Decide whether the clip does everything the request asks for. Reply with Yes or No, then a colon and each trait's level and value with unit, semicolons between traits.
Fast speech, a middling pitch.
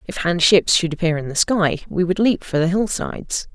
Yes: fast, 235 wpm; medium, 175 Hz